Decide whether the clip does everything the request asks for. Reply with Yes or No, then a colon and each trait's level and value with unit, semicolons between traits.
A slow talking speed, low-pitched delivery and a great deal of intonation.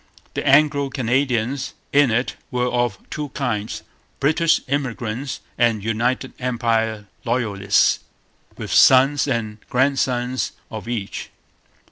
No: slow, 105 wpm; low, 125 Hz; average, 3.2 semitones